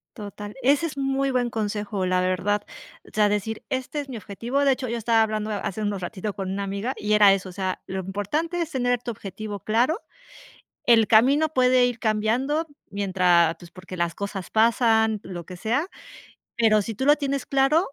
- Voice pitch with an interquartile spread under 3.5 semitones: No, average, 4.4 semitones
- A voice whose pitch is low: No, high, 220 Hz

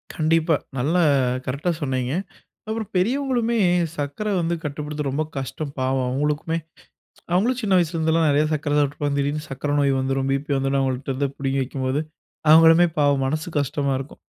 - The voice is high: No, medium, 145 Hz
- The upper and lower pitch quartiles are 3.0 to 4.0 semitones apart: Yes, average, 3.3 semitones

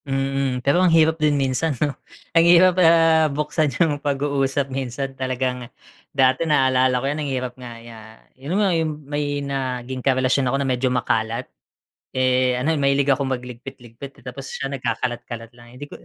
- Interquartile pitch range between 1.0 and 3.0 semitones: Yes, narrow, 2.4 semitones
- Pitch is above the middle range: No, low, 135 Hz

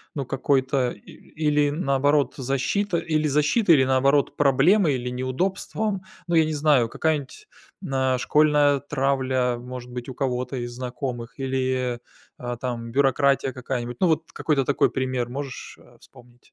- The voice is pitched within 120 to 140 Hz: Yes, low, 135 Hz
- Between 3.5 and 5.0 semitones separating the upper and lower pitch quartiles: No, average, 2.9 semitones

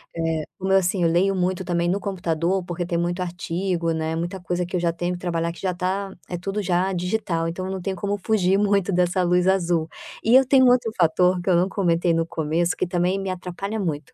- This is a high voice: No, medium, 180 Hz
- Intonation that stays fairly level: Yes, narrow, 2.0 semitones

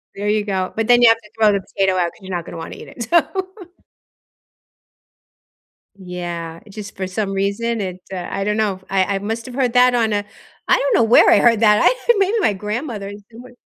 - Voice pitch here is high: Yes, high, 210 Hz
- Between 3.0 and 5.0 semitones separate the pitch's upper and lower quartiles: Yes, average, 3.3 semitones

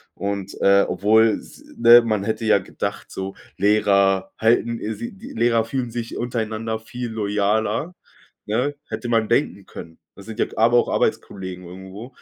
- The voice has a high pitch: No, low, 110 Hz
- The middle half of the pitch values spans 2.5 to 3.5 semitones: Yes, average, 2.9 semitones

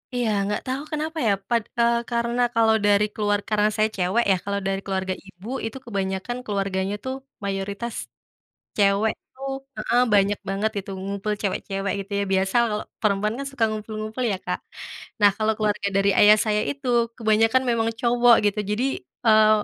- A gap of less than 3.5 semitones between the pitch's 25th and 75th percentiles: Yes, average, 2.9 semitones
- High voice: Yes, high, 215 Hz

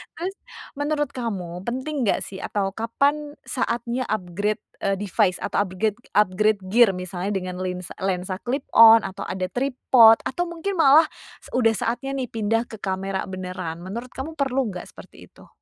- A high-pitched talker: Yes, high, 220 Hz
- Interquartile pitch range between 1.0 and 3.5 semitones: No, wide, 5.4 semitones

